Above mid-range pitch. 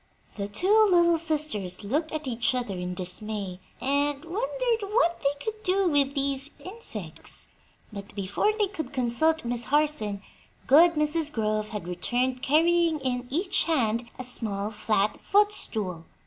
Yes: very high, 275 Hz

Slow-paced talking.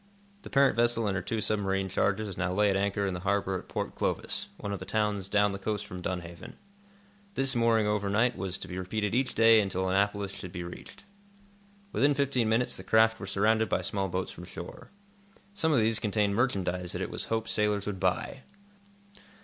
No: average, 200 wpm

